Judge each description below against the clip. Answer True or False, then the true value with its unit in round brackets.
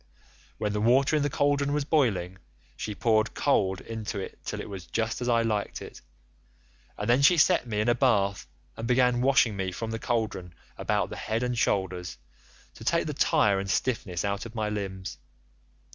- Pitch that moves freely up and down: False (3.9 semitones)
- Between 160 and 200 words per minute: True (190 wpm)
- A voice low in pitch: True (110 Hz)